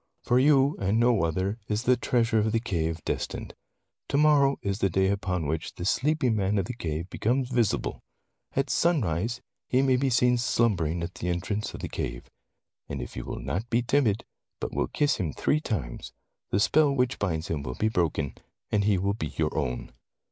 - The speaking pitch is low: Yes, low, 105 Hz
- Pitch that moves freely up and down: Yes, wide, 6.4 semitones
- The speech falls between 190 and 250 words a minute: Yes, average, 200 wpm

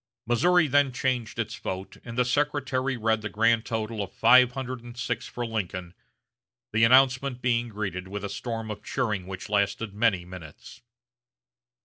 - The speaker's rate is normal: Yes, average, 160 wpm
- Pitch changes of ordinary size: Yes, average, 3.6 semitones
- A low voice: Yes, low, 115 Hz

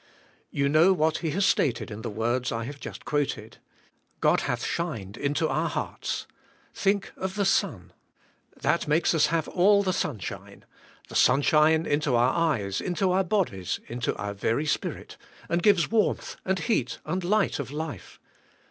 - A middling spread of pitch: No, wide, 6.8 semitones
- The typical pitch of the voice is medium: Yes, medium, 155 Hz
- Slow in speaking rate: No, average, 165 wpm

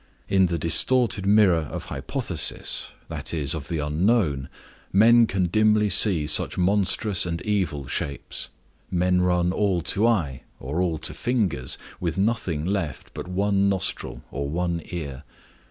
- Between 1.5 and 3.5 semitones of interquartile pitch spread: No, average, 4.3 semitones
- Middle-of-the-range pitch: No, very low, 90 Hz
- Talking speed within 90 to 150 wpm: Yes, average, 145 wpm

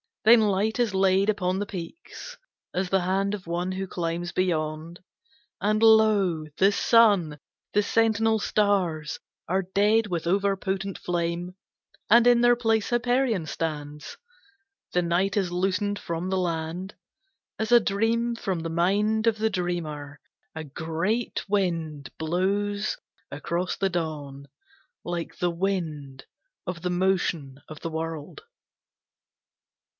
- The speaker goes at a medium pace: No, slow, 130 wpm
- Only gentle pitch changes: No, average, 3.8 semitones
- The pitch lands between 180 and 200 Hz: Yes, medium, 185 Hz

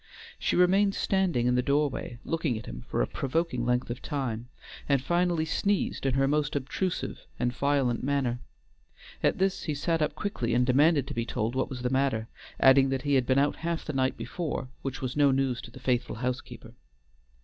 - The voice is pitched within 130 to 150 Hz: Yes, low, 135 Hz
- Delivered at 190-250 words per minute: Yes, average, 200 wpm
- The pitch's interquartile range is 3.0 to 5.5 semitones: Yes, average, 3.5 semitones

